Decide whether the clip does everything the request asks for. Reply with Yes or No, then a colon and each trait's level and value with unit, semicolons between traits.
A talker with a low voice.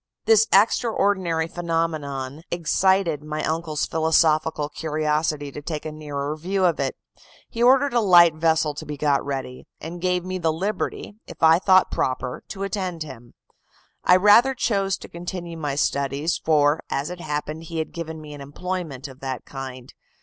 No: medium, 160 Hz